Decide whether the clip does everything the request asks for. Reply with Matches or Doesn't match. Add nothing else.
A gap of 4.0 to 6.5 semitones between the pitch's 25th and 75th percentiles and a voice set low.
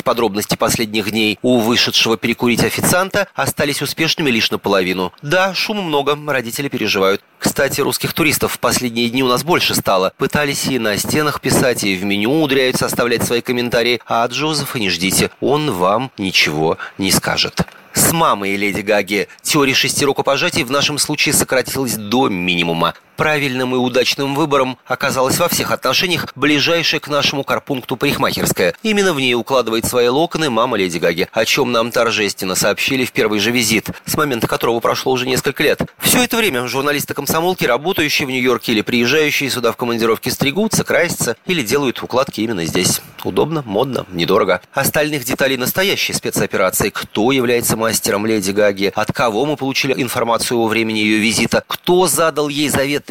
Matches